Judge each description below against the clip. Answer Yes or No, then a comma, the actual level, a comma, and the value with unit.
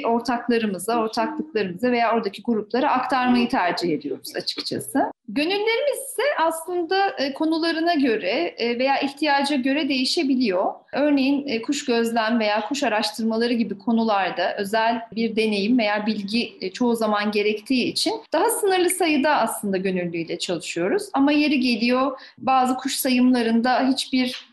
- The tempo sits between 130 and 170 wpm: No, average, 115 wpm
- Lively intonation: No, average, 4.3 semitones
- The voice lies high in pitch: Yes, high, 245 Hz